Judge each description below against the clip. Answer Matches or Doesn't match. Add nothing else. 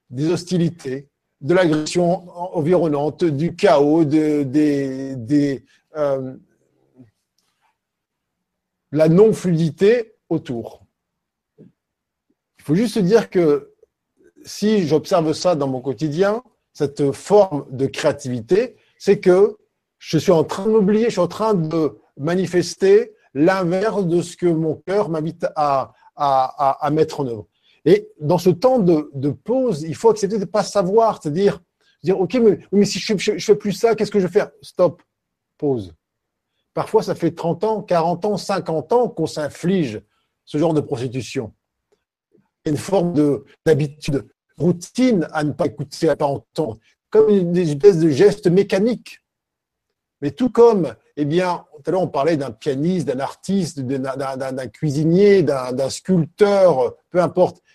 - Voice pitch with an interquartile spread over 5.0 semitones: Matches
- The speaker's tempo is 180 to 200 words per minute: Doesn't match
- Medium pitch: Matches